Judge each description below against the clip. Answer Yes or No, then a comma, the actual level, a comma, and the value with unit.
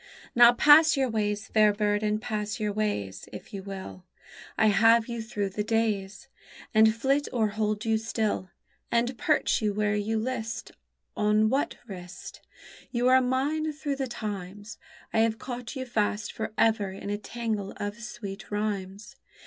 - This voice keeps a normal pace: Yes, average, 165 wpm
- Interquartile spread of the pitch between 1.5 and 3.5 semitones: Yes, narrow, 2.4 semitones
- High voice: Yes, high, 215 Hz